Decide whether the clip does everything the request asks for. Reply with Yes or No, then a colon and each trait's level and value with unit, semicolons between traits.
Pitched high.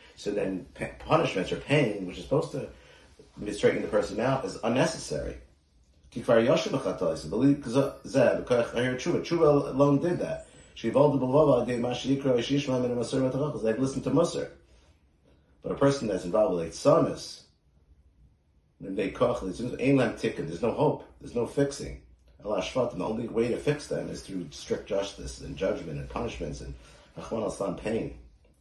No: low, 115 Hz